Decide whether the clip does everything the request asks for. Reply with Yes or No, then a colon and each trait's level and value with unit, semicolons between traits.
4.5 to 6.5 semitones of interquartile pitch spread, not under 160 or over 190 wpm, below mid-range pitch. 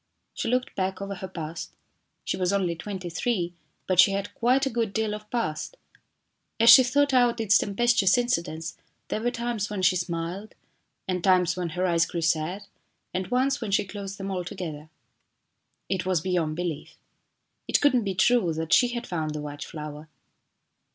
No: average, 5.1 semitones; average, 180 wpm; high, 190 Hz